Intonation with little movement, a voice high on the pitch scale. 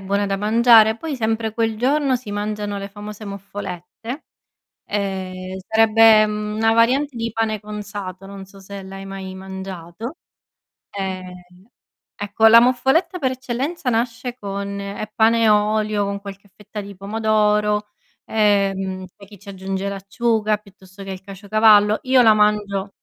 Yes: narrow, 2.3 semitones; high, 210 Hz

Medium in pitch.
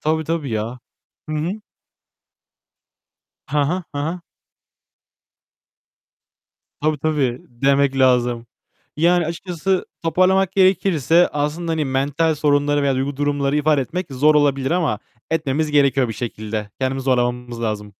Yes: medium, 145 Hz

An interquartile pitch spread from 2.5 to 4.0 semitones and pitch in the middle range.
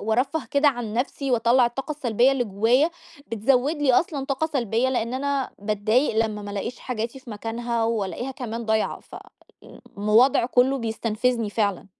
No: average, 3.3 semitones; high, 240 Hz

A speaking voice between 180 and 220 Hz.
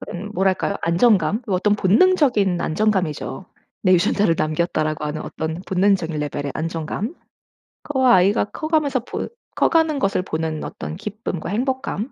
Yes: high, 190 Hz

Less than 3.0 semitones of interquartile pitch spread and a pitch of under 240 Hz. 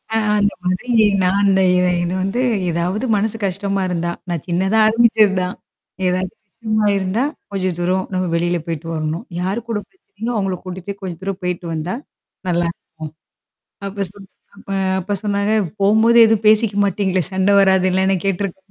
Yes: narrow, 2.4 semitones; high, 190 Hz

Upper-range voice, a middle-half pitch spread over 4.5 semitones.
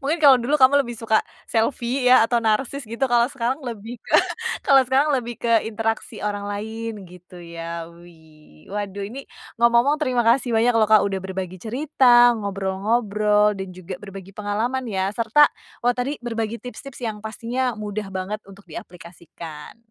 No: high, 220 Hz; average, 3.8 semitones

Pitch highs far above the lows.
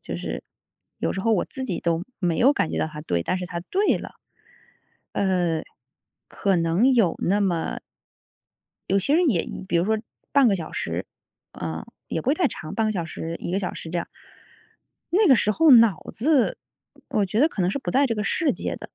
Yes: wide, 7.0 semitones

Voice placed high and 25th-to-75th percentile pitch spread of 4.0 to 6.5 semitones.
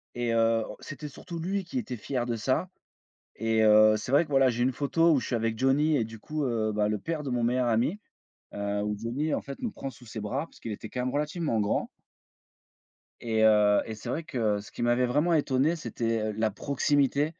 No: low, 120 Hz; average, 4.9 semitones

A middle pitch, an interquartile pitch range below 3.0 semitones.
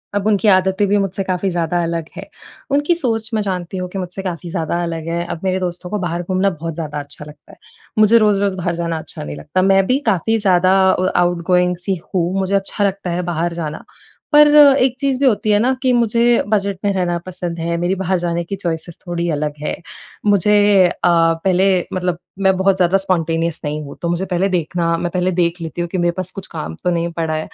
Yes: medium, 180 Hz; narrow, 2.6 semitones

